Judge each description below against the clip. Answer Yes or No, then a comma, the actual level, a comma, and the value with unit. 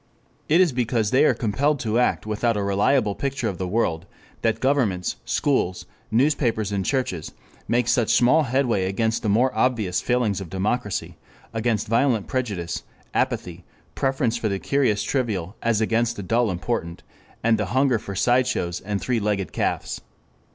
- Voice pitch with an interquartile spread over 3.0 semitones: Yes, average, 4.0 semitones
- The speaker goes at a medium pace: Yes, average, 160 wpm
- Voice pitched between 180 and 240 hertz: No, low, 115 Hz